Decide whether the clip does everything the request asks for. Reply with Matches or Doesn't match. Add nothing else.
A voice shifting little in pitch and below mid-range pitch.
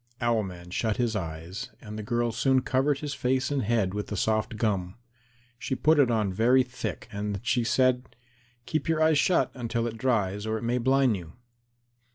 Doesn't match